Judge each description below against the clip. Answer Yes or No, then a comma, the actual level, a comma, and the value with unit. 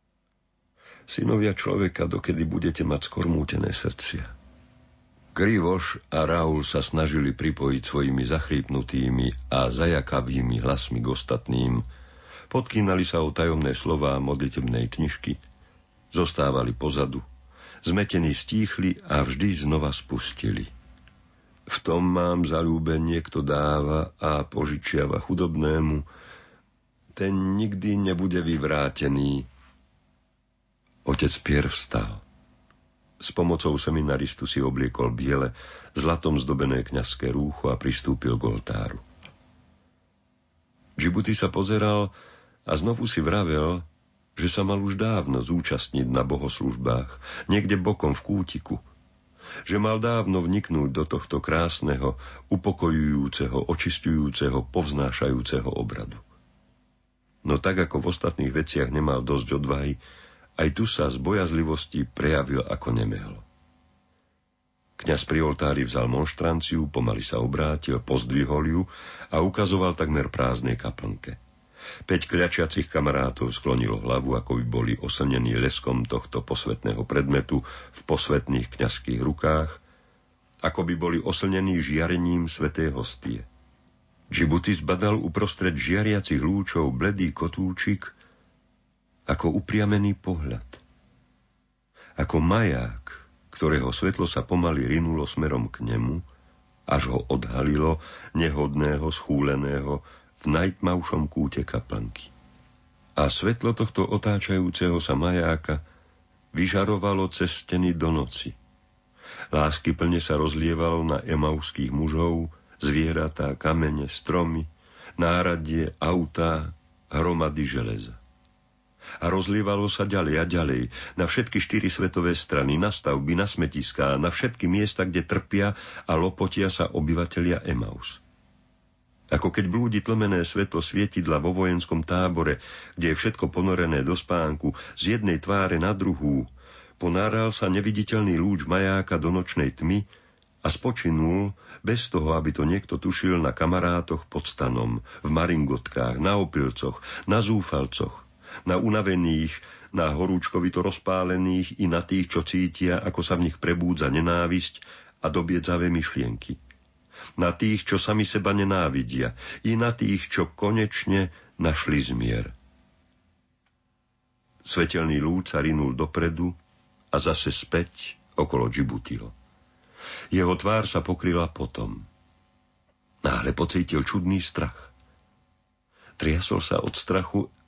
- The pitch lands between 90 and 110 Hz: No, very low, 80 Hz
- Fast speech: No, slow, 110 wpm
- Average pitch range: Yes, average, 4.8 semitones